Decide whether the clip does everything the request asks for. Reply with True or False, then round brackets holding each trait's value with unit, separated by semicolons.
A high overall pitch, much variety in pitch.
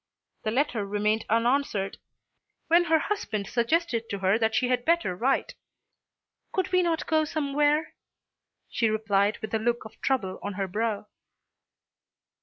True (230 Hz; 6.1 semitones)